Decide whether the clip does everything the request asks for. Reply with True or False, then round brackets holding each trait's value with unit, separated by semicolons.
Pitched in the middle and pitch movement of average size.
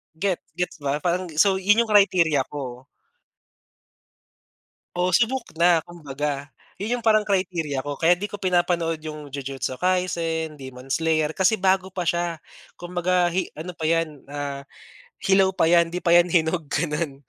True (170 Hz; 3.5 semitones)